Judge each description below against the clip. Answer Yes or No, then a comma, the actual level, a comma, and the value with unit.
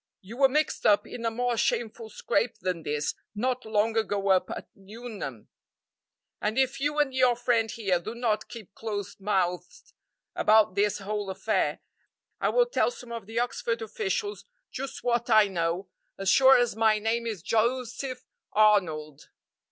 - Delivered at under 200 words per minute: Yes, average, 160 wpm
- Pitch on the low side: No, high, 225 Hz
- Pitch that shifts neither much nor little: Yes, average, 3.7 semitones